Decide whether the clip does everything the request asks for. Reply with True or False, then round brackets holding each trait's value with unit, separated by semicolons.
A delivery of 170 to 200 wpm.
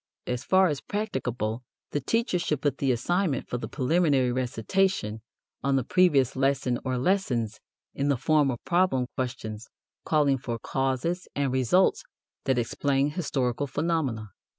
False (145 wpm)